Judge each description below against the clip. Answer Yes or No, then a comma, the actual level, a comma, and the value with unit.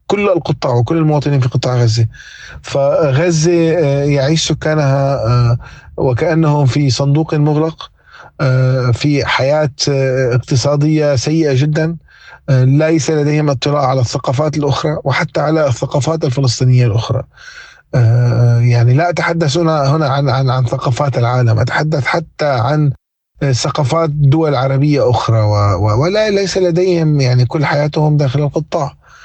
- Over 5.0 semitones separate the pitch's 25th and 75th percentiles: No, average, 3.4 semitones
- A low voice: No, medium, 145 Hz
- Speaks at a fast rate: No, average, 110 wpm